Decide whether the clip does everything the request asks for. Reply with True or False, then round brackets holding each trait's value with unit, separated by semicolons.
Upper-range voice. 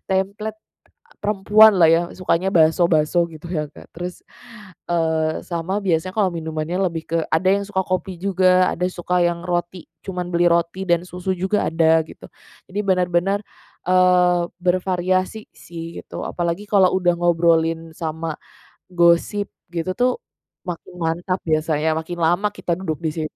False (175 Hz)